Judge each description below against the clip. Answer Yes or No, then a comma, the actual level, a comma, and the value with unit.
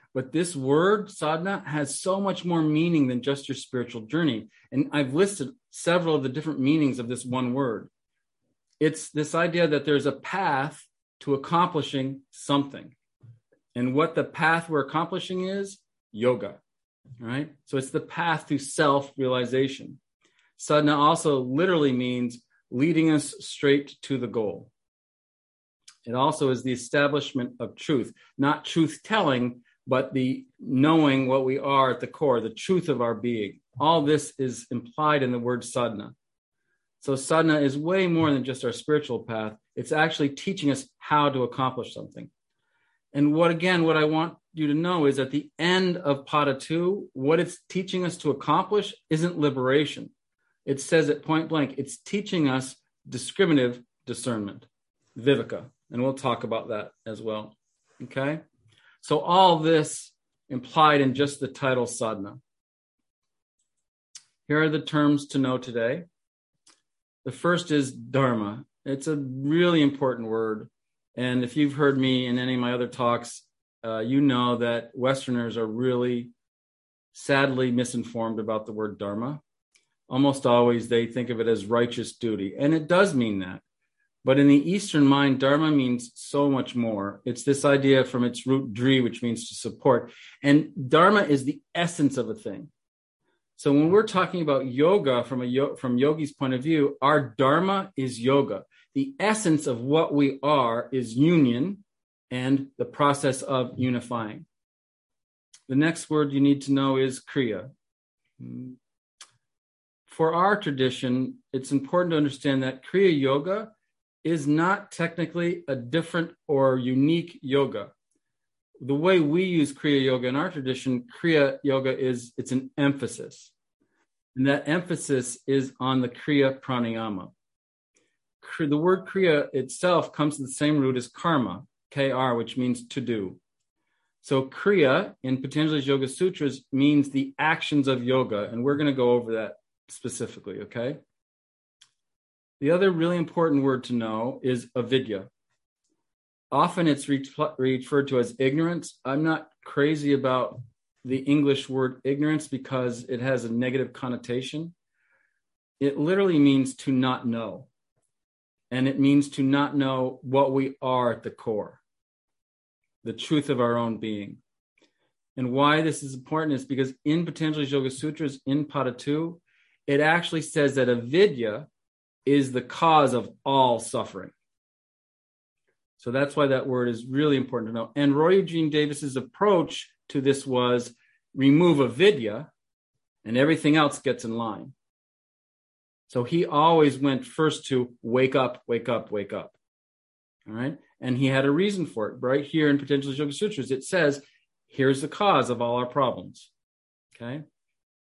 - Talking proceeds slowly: No, average, 155 wpm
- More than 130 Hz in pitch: Yes, medium, 140 Hz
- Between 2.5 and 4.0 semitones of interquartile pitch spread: Yes, average, 3.4 semitones